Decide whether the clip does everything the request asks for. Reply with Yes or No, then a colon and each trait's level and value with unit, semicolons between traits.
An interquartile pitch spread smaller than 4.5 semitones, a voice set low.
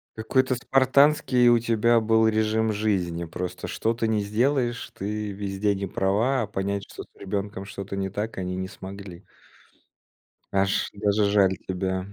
Yes: average, 2.7 semitones; low, 105 Hz